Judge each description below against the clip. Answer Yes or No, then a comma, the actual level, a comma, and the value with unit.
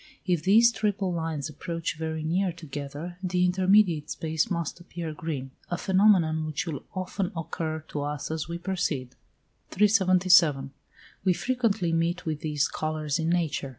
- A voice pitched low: No, medium, 170 Hz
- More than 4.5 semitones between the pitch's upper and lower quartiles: No, average, 3.0 semitones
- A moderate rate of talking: Yes, average, 150 wpm